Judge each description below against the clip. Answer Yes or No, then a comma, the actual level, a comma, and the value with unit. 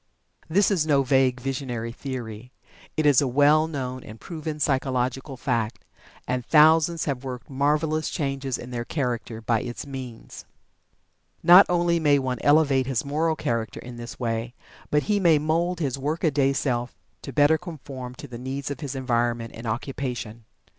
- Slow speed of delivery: No, average, 165 wpm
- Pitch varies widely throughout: No, average, 3.7 semitones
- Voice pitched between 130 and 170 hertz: Yes, low, 135 Hz